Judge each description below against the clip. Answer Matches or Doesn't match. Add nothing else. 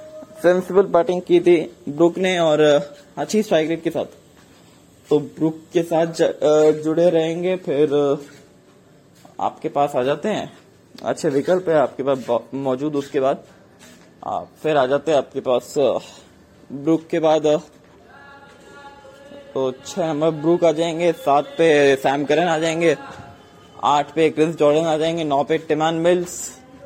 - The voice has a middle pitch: Matches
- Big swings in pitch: Doesn't match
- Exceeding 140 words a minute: Doesn't match